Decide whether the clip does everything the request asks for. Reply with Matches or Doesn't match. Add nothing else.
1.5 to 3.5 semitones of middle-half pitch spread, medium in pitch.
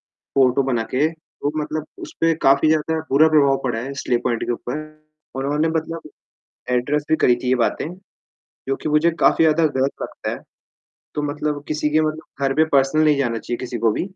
Matches